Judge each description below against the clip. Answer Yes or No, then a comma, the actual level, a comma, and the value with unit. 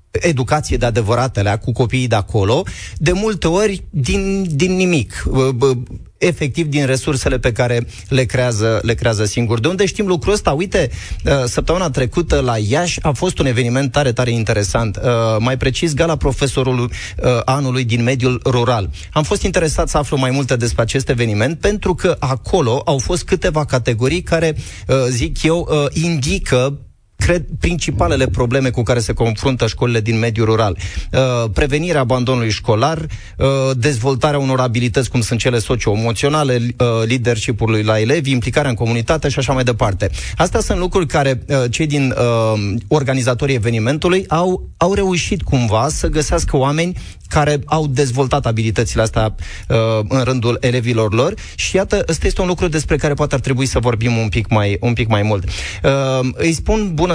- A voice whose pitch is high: No, low, 130 Hz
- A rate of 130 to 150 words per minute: No, average, 160 wpm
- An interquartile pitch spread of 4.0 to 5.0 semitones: Yes, average, 4.5 semitones